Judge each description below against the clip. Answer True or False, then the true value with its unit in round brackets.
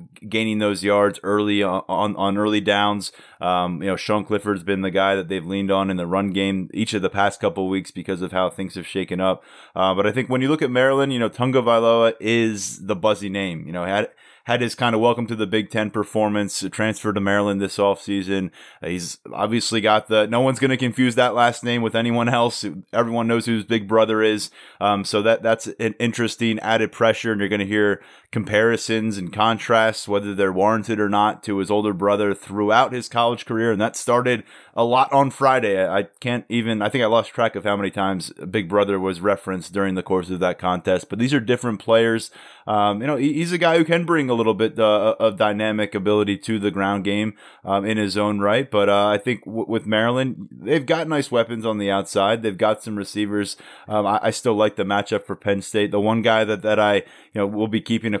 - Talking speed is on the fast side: True (230 wpm)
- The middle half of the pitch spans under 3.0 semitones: True (2.5 semitones)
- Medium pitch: False (105 Hz)